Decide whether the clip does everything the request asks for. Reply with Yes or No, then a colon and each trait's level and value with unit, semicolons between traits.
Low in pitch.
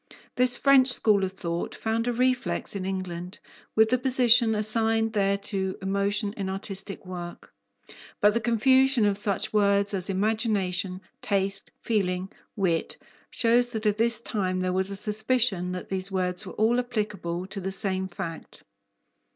No: high, 200 Hz